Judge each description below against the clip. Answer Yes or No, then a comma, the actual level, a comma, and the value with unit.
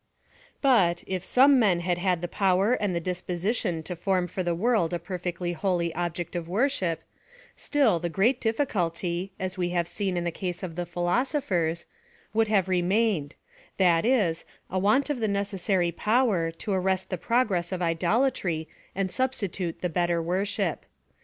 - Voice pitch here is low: No, medium, 185 Hz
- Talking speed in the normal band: Yes, average, 165 wpm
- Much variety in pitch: No, average, 3.3 semitones